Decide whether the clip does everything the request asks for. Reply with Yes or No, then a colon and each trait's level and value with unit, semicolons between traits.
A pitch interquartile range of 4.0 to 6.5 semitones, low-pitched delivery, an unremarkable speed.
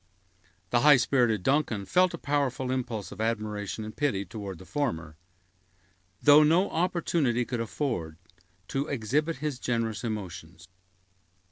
No: wide, 5.6 semitones; low, 120 Hz; slow, 130 wpm